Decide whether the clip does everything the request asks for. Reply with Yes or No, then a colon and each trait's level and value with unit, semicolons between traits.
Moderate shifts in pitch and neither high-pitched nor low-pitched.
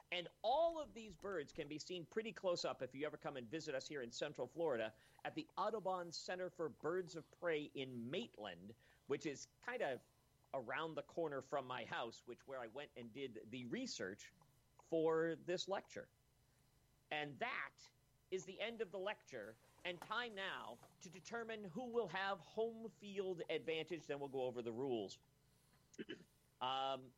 No: wide, 6.1 semitones; medium, 160 Hz